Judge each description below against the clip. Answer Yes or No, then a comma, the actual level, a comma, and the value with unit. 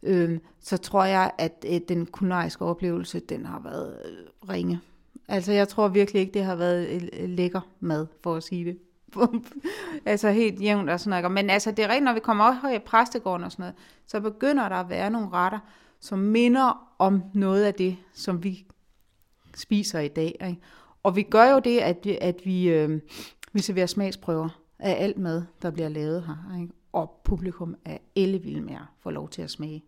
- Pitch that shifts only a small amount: No, average, 3.4 semitones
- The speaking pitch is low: No, medium, 185 Hz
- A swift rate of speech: No, average, 195 wpm